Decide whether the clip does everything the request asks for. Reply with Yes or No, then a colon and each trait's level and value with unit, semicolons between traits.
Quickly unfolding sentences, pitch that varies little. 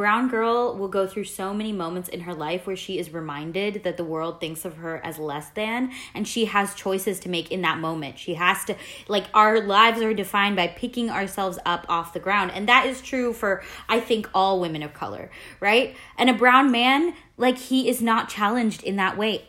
No: fast, 220 wpm; average, 4.3 semitones